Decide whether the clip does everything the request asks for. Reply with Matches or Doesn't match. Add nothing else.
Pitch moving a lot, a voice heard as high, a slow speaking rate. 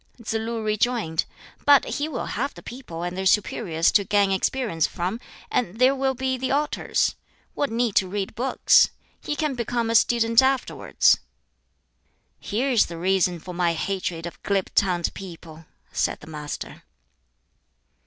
Doesn't match